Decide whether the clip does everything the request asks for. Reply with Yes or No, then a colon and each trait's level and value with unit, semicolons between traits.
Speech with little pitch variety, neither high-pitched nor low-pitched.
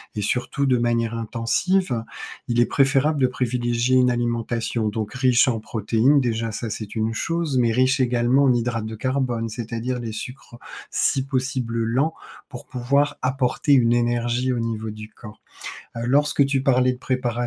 No: narrow, 2.1 semitones; low, 120 Hz